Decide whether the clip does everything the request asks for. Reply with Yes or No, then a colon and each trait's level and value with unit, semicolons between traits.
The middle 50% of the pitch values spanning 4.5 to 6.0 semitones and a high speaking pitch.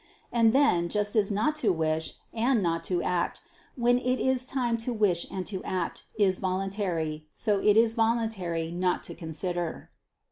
Yes: average, 4.9 semitones; high, 200 Hz